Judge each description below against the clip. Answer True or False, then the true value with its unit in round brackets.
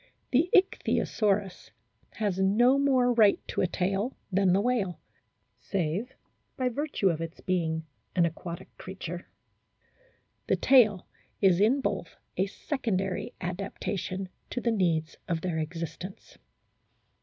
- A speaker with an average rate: False (120 wpm)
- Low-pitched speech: False (195 Hz)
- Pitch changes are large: False (4.7 semitones)